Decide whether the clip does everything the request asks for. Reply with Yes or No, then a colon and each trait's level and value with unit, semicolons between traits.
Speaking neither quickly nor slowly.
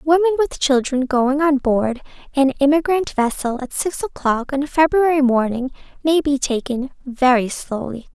Yes: average, 155 wpm